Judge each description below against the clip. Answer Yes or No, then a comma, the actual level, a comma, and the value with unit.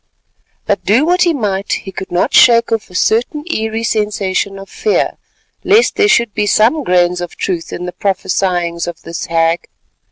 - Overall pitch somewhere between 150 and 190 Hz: No, high, 200 Hz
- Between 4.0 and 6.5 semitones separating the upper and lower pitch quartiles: Yes, average, 4.7 semitones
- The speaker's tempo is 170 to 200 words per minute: Yes, average, 180 wpm